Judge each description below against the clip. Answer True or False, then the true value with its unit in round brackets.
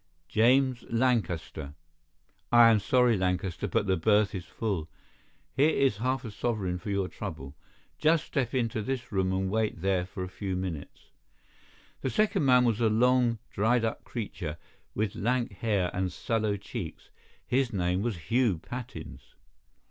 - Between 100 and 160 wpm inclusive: True (155 wpm)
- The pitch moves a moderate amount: True (4.8 semitones)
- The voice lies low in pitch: True (110 Hz)